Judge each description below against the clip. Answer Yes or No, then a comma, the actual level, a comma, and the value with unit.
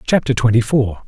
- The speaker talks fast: No, average, 170 wpm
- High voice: No, low, 120 Hz